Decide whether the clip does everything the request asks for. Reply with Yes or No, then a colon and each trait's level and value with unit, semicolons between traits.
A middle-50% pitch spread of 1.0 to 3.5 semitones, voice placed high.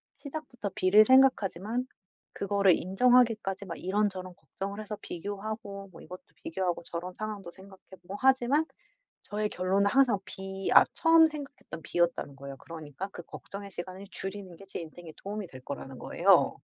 Yes: average, 2.9 semitones; high, 195 Hz